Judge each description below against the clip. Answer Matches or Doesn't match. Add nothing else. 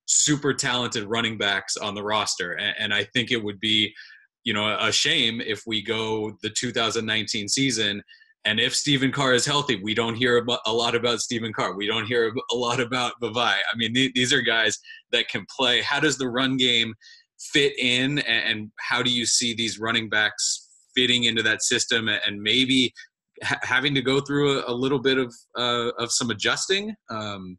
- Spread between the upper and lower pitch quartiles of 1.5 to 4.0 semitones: Matches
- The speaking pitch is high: Doesn't match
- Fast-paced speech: Doesn't match